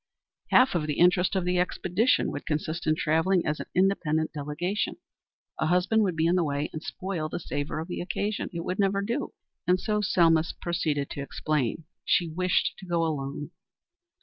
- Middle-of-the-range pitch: Yes, medium, 170 Hz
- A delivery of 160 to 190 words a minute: Yes, average, 185 wpm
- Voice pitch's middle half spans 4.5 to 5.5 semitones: No, average, 3.1 semitones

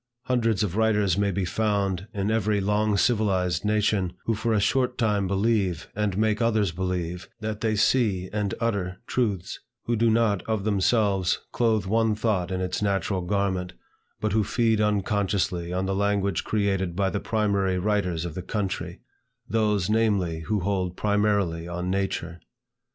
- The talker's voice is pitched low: Yes, low, 100 Hz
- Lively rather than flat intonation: No, average, 2.7 semitones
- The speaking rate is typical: Yes, average, 160 wpm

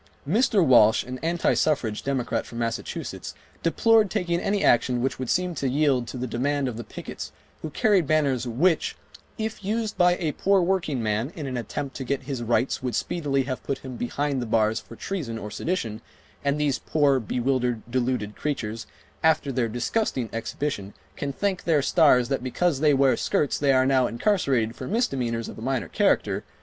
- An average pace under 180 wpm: No, average, 185 wpm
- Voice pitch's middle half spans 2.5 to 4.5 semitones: No, average, 4.9 semitones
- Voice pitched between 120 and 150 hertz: Yes, low, 135 Hz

